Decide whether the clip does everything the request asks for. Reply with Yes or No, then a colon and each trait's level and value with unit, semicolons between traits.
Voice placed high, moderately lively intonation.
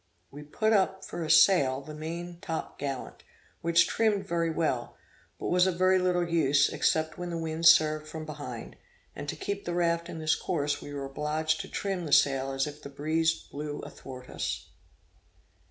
No: medium, 160 Hz; average, 3.0 semitones